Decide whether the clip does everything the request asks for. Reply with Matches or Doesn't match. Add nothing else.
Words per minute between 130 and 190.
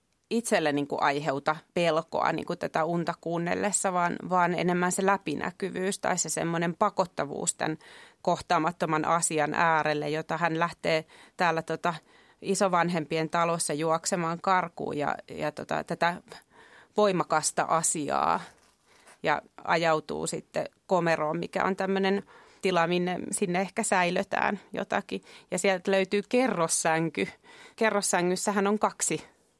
Doesn't match